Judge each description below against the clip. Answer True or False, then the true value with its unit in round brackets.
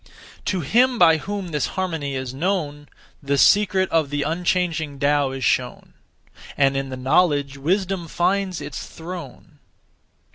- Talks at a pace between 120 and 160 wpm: True (140 wpm)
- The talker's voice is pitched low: False (160 Hz)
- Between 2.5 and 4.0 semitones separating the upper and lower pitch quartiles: False (4.7 semitones)